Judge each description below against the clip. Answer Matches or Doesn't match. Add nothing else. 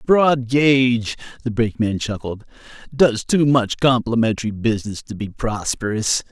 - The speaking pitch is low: Matches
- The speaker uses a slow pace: Matches